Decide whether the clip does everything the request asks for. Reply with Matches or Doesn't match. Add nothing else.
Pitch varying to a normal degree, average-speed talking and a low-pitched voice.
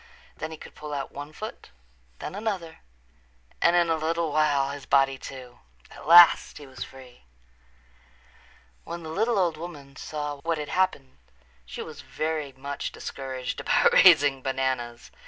Doesn't match